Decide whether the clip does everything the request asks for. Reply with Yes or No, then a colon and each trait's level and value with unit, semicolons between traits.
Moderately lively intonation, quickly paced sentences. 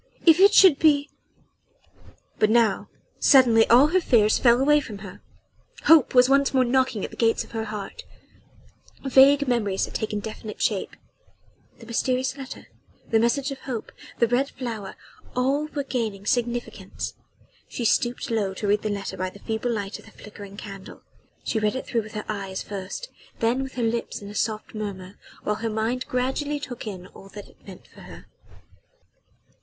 No: average, 3.9 semitones; average, 180 wpm